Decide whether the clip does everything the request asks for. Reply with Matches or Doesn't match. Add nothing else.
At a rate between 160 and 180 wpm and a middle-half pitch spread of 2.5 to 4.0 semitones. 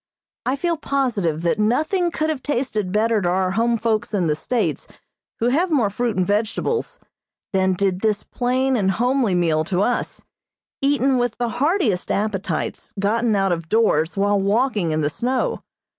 Doesn't match